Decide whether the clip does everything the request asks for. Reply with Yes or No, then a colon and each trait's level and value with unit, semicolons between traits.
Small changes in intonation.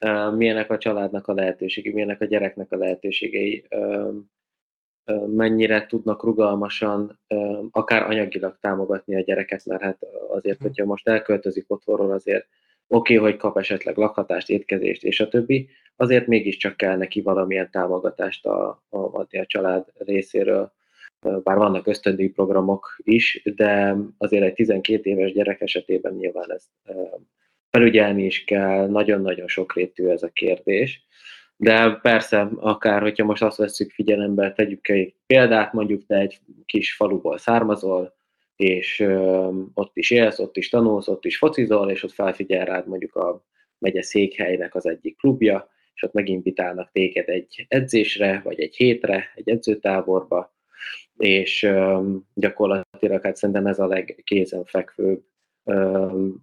Yes: narrow, 2.1 semitones